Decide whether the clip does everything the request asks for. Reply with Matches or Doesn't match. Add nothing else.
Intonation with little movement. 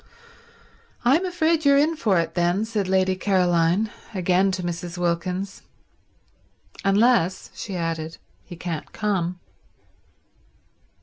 Doesn't match